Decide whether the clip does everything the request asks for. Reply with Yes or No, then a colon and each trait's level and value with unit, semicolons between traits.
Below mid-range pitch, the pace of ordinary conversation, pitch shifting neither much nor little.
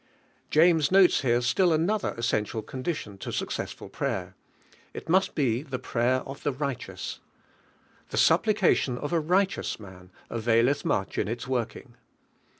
No: low, 130 Hz; average, 145 wpm; wide, 5.8 semitones